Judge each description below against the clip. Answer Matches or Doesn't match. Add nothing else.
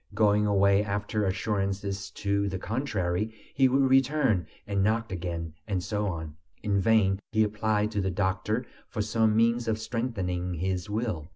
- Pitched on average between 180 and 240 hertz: Doesn't match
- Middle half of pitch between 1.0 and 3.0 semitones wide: Matches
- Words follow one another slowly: Doesn't match